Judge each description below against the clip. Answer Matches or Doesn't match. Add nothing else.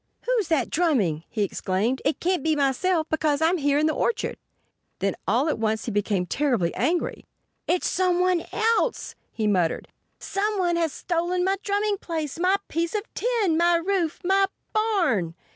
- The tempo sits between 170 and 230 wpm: Doesn't match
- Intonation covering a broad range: Matches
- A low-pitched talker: Doesn't match